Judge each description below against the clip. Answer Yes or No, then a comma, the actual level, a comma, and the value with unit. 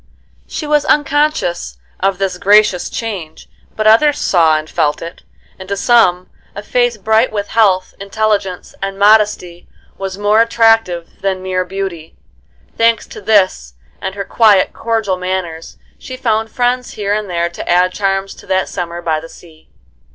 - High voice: Yes, high, 195 Hz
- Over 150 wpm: Yes, average, 160 wpm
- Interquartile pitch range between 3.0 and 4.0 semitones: Yes, average, 3.5 semitones